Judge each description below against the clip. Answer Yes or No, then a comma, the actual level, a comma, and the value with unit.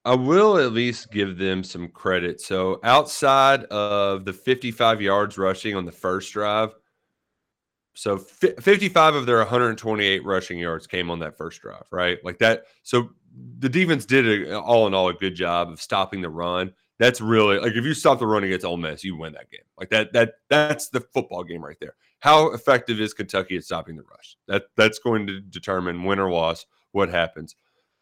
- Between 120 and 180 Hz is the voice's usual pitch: No, low, 100 Hz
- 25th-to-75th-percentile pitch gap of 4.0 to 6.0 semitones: Yes, average, 4.7 semitones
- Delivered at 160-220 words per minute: Yes, average, 195 wpm